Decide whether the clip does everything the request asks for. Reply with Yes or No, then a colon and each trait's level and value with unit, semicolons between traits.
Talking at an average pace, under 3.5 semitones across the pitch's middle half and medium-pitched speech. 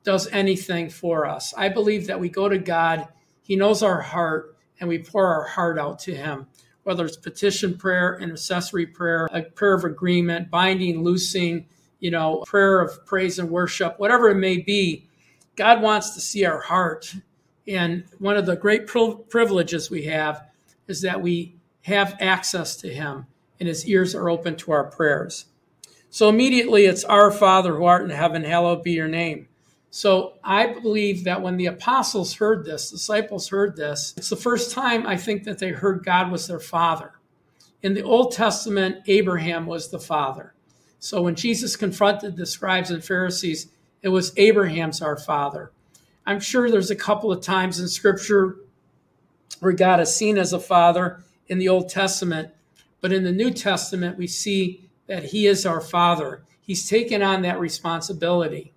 Yes: average, 175 wpm; average, 2.9 semitones; medium, 180 Hz